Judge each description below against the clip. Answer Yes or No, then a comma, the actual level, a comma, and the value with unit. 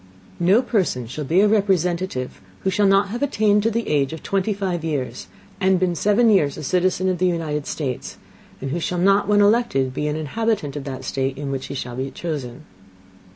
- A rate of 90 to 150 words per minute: No, fast, 205 wpm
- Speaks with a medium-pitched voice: Yes, medium, 175 Hz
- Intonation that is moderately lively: No, wide, 6.1 semitones